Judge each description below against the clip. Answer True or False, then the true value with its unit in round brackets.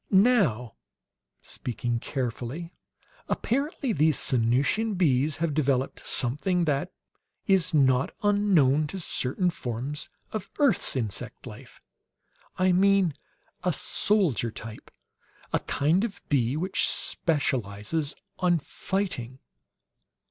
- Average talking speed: False (100 wpm)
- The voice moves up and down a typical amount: False (6.8 semitones)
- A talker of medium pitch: True (155 Hz)